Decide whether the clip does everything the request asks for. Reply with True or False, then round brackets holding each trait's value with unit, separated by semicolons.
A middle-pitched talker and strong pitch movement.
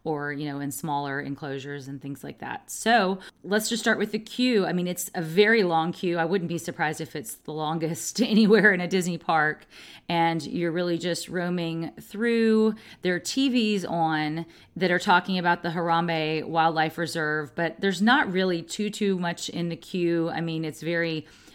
False (170 Hz; 3.5 semitones)